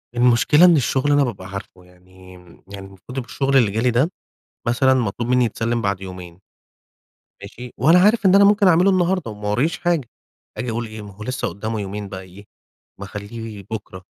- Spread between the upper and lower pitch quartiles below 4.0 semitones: No, wide, 5.5 semitones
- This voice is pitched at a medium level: No, low, 115 Hz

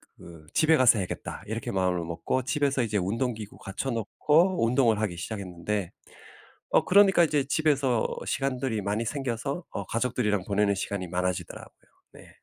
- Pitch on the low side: Yes, low, 115 Hz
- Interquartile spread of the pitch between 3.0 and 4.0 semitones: No, wide, 5.5 semitones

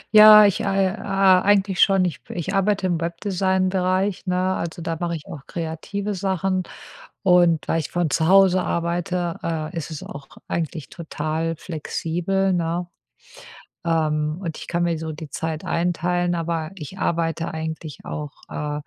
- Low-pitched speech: No, medium, 170 Hz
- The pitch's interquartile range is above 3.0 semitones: No, narrow, 2.6 semitones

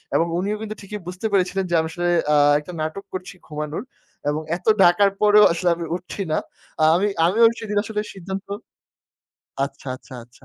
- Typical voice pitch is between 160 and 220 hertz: Yes, medium, 185 Hz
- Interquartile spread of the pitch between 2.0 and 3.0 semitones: No, average, 3.6 semitones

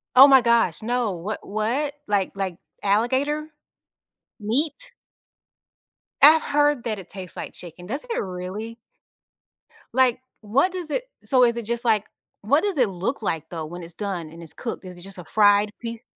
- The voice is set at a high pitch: Yes, high, 220 Hz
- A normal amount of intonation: No, wide, 5.8 semitones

